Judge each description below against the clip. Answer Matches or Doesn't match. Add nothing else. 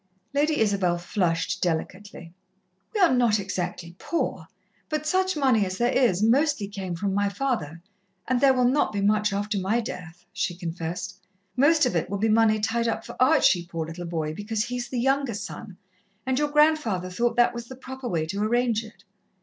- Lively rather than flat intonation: Matches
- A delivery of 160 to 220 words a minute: Matches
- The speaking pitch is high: Matches